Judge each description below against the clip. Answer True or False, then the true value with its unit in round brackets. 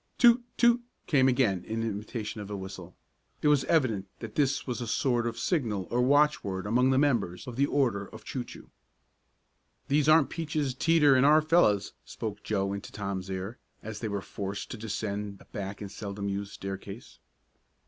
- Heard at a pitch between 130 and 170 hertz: False (110 Hz)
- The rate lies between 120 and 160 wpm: False (180 wpm)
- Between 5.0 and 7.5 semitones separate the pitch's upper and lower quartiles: True (5.6 semitones)